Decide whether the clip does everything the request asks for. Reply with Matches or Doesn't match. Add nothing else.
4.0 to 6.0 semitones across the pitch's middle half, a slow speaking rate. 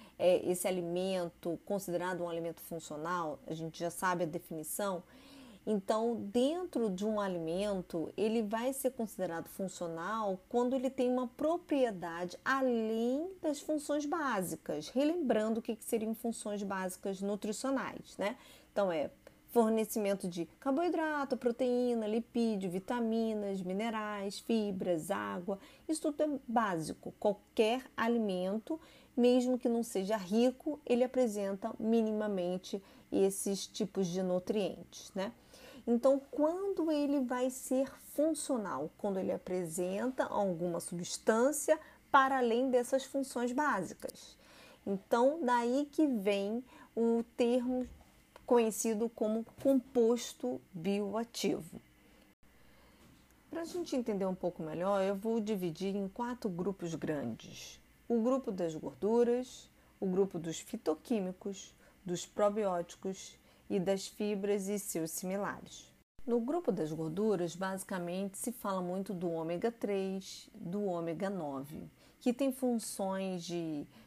Matches